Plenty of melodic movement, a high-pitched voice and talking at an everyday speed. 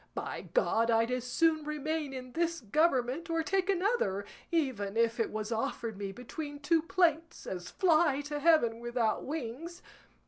Yes: wide, 6.1 semitones; very high, 285 Hz; average, 160 wpm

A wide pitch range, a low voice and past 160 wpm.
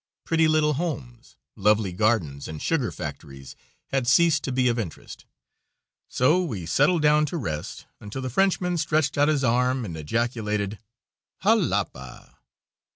No: wide, 6.9 semitones; low, 125 Hz; average, 140 wpm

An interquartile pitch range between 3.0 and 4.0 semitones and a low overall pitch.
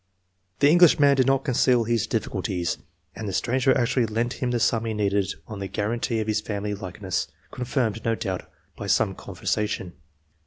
Yes: average, 3.4 semitones; low, 115 Hz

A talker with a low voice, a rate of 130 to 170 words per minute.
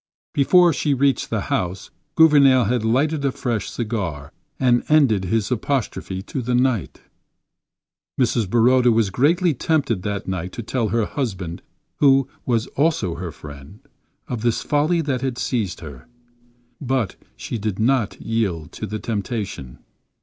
Yes: low, 120 Hz; average, 140 wpm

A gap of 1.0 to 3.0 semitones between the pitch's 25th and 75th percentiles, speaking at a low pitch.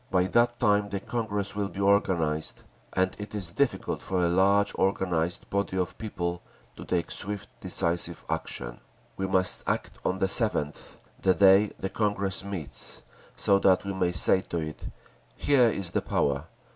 Yes: narrow, 2.5 semitones; very low, 95 Hz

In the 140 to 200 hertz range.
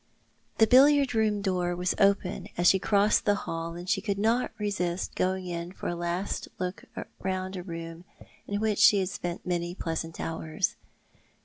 Yes: medium, 185 Hz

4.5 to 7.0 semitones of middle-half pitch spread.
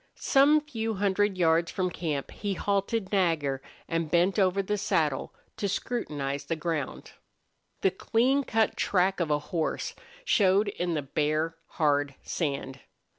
Yes: average, 4.9 semitones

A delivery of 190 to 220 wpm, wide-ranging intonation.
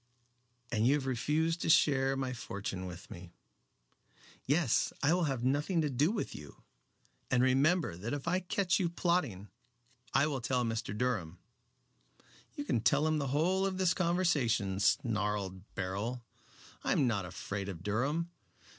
No: average, 155 wpm; wide, 7.3 semitones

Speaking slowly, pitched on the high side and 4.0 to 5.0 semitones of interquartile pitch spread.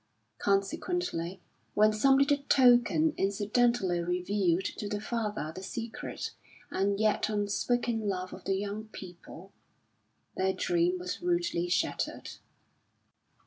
Yes: slow, 110 wpm; high, 205 Hz; average, 4.3 semitones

